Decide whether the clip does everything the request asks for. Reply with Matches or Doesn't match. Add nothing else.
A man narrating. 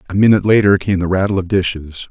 Matches